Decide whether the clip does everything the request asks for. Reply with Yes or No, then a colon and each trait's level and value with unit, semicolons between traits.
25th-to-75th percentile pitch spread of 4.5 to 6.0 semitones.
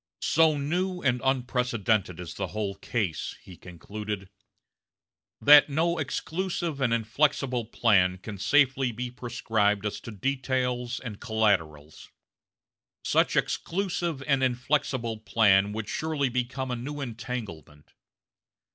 Yes: average, 4.8 semitones